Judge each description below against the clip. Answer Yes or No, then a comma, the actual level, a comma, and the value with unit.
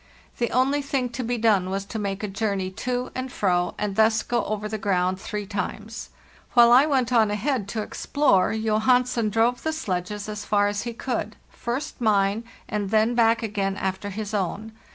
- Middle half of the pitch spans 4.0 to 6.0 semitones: No, average, 3.1 semitones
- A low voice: No, high, 215 Hz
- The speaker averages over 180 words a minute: Yes, average, 190 wpm